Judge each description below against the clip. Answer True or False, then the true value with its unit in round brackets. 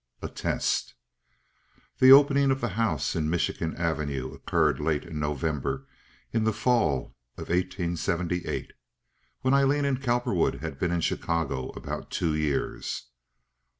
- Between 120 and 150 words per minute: True (140 wpm)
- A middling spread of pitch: False (8.0 semitones)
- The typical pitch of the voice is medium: False (85 Hz)